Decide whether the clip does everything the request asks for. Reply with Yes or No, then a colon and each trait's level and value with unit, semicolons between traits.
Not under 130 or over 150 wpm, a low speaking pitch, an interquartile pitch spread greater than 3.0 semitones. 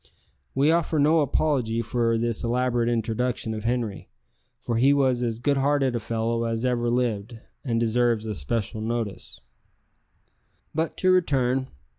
No: average, 140 wpm; low, 120 Hz; narrow, 2.6 semitones